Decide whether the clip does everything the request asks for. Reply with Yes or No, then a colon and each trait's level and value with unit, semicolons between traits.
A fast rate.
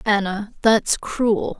No: slow, 115 wpm